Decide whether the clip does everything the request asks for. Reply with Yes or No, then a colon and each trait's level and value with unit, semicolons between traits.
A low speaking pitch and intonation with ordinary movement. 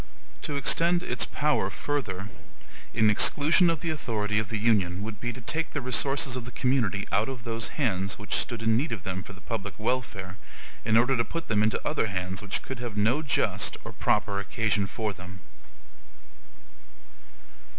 Yes: low, 115 Hz; average, 4.6 semitones